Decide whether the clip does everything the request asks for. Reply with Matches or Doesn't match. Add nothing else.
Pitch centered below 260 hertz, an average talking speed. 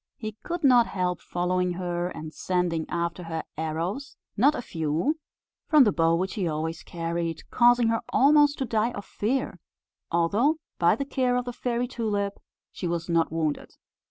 Matches